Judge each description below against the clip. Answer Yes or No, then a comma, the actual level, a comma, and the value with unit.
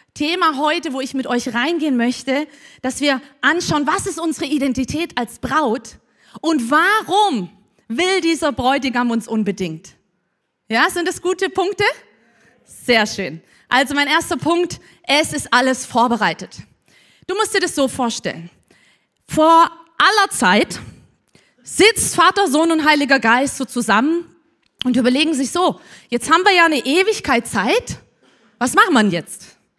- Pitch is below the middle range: No, very high, 290 Hz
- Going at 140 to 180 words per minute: Yes, average, 145 wpm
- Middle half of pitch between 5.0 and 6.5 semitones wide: Yes, wide, 5.5 semitones